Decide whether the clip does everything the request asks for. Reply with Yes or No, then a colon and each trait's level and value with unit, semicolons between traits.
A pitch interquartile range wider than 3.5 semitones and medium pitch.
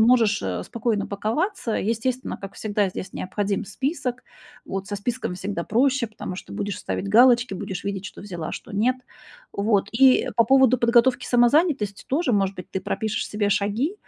No: average, 3.9 semitones; high, 215 Hz